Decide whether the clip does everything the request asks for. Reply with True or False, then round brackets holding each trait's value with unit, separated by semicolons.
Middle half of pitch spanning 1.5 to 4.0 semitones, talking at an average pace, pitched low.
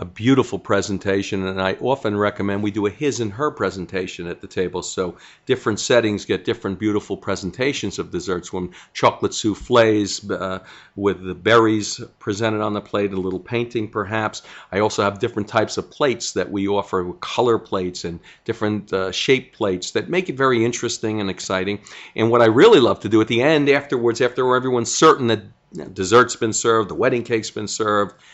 True (3.3 semitones; 185 wpm; 105 Hz)